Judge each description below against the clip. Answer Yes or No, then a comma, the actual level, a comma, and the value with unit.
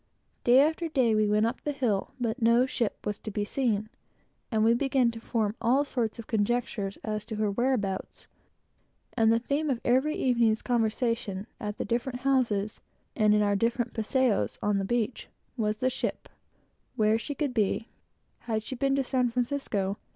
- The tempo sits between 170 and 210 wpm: Yes, average, 180 wpm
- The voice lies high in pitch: Yes, high, 230 Hz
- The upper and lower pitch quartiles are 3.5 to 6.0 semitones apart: No, average, 3.1 semitones